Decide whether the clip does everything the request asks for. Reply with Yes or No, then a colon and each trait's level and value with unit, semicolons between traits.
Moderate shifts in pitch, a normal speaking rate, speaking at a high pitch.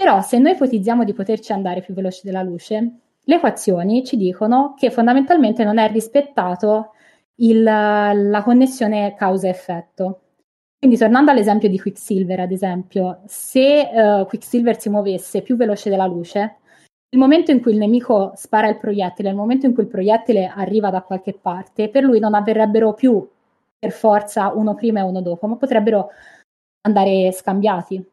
Yes: average, 3.2 semitones; average, 160 wpm; high, 215 Hz